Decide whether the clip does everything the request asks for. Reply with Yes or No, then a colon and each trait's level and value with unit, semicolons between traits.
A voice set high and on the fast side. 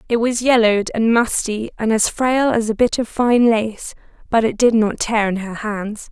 Yes: high, 225 Hz; fast, 215 wpm